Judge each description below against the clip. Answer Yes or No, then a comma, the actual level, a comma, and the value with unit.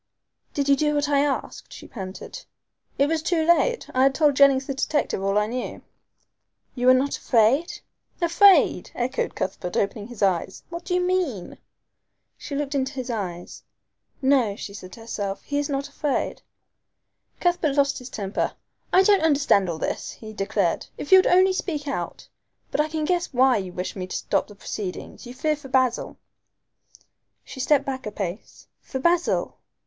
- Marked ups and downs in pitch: Yes, wide, 6.1 semitones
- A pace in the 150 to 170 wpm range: No, average, 180 wpm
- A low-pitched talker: No, very high, 270 Hz